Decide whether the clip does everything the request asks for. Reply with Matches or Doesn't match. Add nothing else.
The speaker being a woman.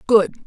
Matches